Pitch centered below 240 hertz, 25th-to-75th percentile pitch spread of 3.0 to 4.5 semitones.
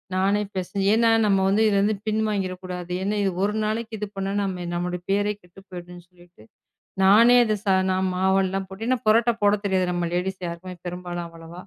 No: high, 190 Hz; narrow, 2.5 semitones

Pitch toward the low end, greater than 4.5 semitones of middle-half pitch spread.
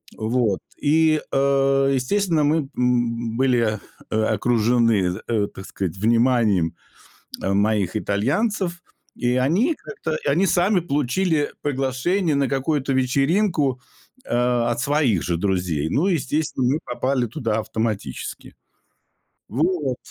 Yes: low, 130 Hz; wide, 5.5 semitones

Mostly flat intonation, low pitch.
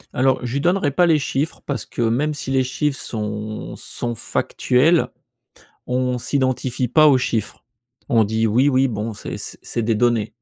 No: average, 3.6 semitones; low, 125 Hz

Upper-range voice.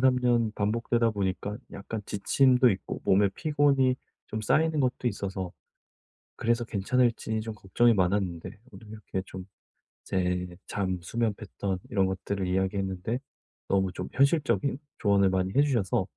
No: low, 105 Hz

